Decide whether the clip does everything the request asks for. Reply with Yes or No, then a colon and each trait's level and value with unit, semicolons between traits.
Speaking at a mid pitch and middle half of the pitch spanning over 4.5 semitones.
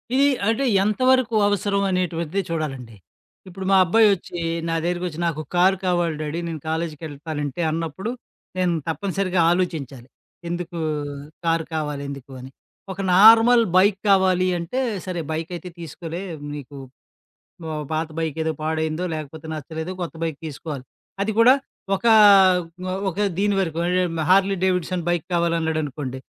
No: medium, 170 Hz; average, 3.2 semitones